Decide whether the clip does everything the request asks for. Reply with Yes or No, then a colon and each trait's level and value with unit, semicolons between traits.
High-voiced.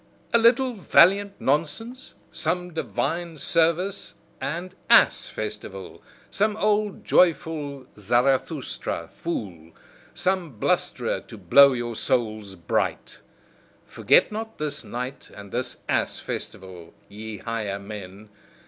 No: medium, 140 Hz